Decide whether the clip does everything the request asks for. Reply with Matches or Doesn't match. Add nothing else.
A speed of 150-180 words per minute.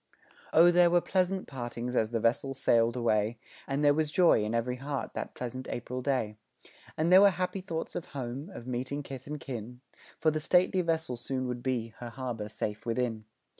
Doesn't match